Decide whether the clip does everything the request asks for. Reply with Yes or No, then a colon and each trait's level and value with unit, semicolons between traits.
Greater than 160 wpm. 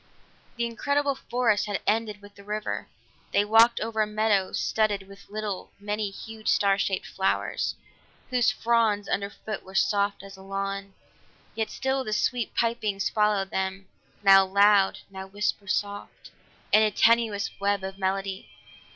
No: average, 150 wpm